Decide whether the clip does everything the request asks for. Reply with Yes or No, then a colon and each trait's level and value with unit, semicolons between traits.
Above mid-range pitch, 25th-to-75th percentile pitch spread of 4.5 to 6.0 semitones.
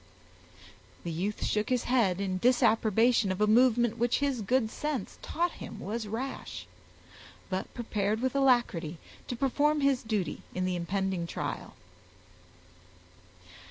Yes: high, 225 Hz; average, 4.8 semitones